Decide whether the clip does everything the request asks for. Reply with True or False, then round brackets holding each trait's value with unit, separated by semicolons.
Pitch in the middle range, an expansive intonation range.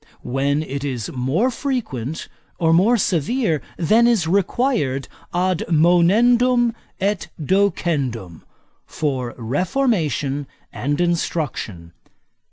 True (165 Hz; 7.3 semitones)